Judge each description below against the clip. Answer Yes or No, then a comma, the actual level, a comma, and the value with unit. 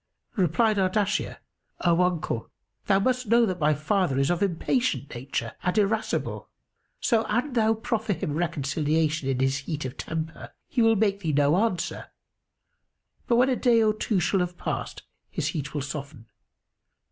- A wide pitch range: Yes, wide, 6.5 semitones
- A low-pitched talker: No, medium, 180 Hz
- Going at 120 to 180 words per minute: Yes, average, 160 wpm